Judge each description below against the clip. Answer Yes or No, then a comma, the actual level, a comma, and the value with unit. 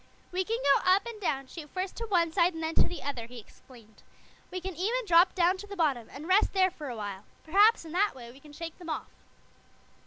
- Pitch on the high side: Yes, very high, 340 Hz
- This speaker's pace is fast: Yes, fast, 245 wpm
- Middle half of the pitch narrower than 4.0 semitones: No, average, 5.3 semitones